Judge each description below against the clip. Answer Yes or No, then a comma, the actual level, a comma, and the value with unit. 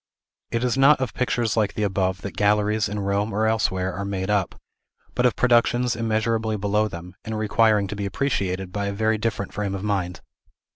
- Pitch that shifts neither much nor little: No, narrow, 2.1 semitones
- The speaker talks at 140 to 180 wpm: No, average, 195 wpm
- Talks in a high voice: No, low, 105 Hz